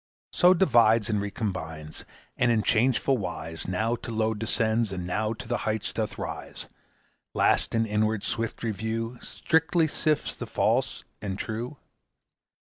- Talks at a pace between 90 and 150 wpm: Yes, average, 140 wpm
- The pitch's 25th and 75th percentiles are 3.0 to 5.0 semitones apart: No, narrow, 2.4 semitones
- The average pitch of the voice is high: No, low, 110 Hz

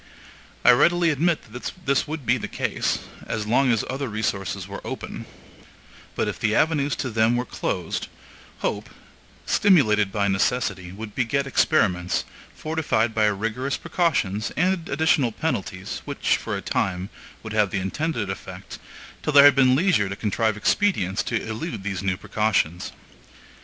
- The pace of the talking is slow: No, average, 150 wpm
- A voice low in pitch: Yes, low, 115 Hz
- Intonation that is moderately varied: No, wide, 5.8 semitones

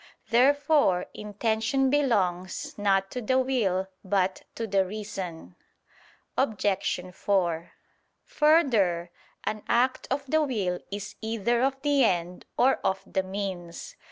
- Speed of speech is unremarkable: No, slow, 120 wpm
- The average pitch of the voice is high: Yes, high, 210 Hz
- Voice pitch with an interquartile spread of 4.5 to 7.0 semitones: Yes, wide, 5.6 semitones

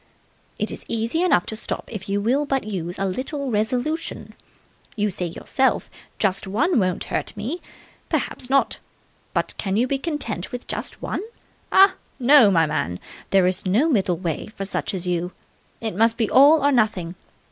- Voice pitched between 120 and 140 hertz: No, high, 220 Hz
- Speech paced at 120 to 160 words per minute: No, average, 180 wpm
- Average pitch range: No, wide, 6.2 semitones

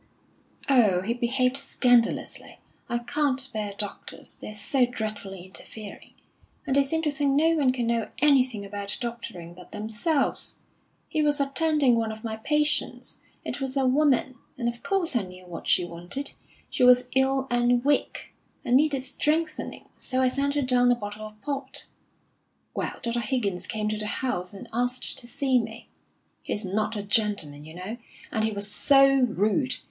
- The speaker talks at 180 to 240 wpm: No, average, 170 wpm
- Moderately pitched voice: No, high, 245 Hz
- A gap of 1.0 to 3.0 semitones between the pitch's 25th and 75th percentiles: No, average, 4.4 semitones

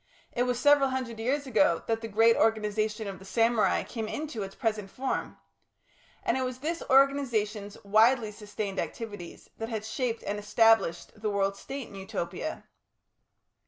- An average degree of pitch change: Yes, average, 3.4 semitones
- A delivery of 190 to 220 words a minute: No, average, 160 wpm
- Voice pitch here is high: Yes, high, 225 Hz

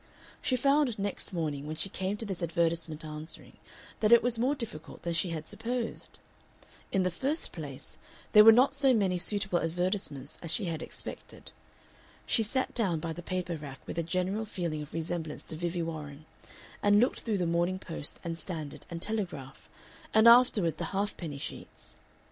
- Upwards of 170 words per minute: Yes, average, 180 wpm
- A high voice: No, medium, 180 Hz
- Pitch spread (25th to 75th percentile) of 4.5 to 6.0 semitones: Yes, average, 4.9 semitones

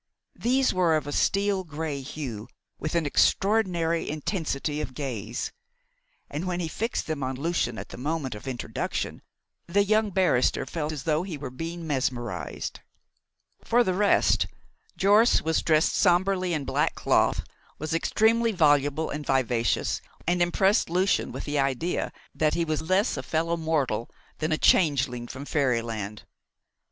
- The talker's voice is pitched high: No, medium, 155 Hz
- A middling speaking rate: Yes, average, 150 wpm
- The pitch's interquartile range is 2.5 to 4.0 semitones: No, average, 4.8 semitones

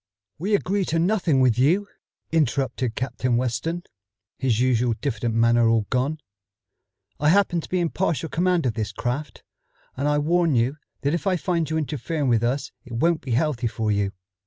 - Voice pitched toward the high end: No, medium, 140 Hz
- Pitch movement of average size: No, wide, 5.7 semitones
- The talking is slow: No, average, 180 wpm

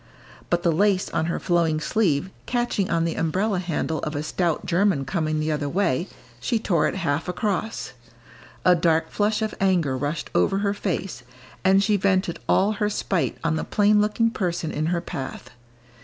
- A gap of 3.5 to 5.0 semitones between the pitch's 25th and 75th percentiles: Yes, average, 4.2 semitones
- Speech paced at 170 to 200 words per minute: Yes, average, 180 wpm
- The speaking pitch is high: No, medium, 180 Hz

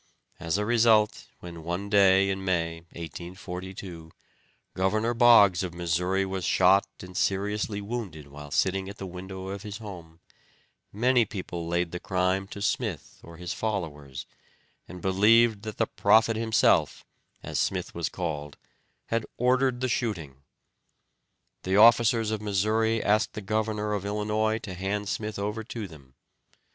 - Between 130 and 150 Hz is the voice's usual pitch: No, low, 100 Hz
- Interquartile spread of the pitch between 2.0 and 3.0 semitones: No, average, 3.4 semitones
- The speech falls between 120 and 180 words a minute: Yes, average, 145 wpm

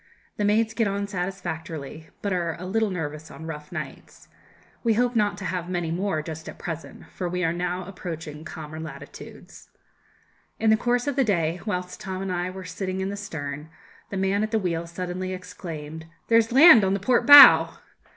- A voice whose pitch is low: No, medium, 185 Hz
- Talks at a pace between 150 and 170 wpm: No, average, 190 wpm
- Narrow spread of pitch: No, average, 3.9 semitones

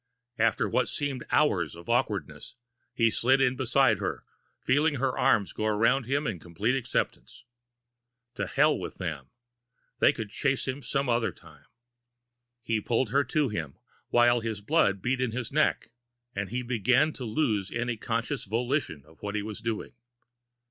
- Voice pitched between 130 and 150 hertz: No, low, 120 Hz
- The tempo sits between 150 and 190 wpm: Yes, average, 160 wpm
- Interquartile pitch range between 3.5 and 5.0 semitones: Yes, average, 3.8 semitones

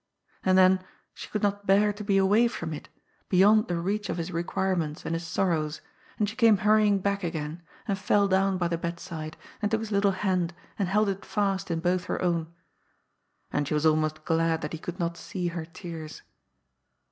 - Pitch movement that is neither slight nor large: Yes, average, 3.3 semitones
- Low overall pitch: No, medium, 185 Hz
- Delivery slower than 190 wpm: No, fast, 205 wpm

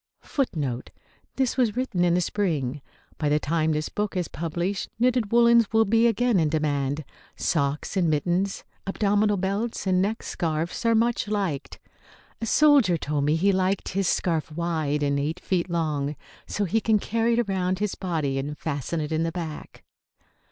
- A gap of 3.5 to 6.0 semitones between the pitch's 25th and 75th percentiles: Yes, average, 5.3 semitones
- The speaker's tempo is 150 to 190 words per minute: Yes, average, 175 wpm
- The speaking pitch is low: No, medium, 180 Hz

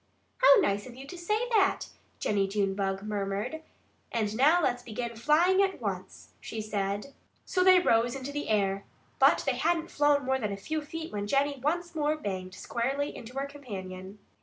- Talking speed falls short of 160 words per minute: No, average, 180 wpm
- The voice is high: Yes, very high, 255 Hz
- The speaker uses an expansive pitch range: Yes, wide, 7.1 semitones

